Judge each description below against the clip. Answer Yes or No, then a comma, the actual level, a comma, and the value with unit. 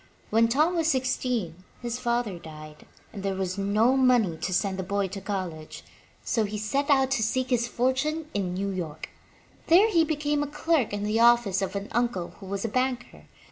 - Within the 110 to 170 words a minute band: No, average, 195 wpm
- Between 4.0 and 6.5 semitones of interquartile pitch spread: Yes, average, 5.1 semitones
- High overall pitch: Yes, high, 225 Hz